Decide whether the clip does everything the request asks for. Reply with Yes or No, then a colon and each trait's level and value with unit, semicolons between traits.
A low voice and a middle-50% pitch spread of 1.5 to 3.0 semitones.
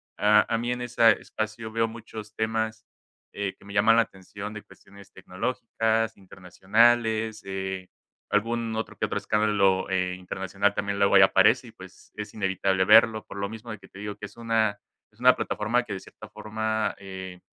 Yes: low, 105 Hz; narrow, 2.4 semitones